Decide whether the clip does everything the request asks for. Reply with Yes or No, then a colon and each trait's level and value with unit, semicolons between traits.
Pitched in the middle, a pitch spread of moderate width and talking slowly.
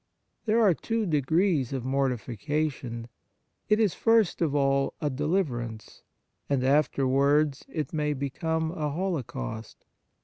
Yes: medium, 145 Hz; average, 3.8 semitones; slow, 130 wpm